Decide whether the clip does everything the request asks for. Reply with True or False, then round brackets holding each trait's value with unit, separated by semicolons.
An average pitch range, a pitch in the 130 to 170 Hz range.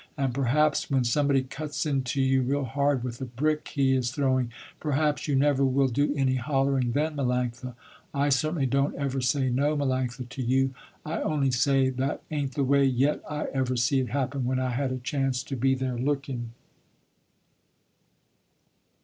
False (1.8 semitones; 135 Hz)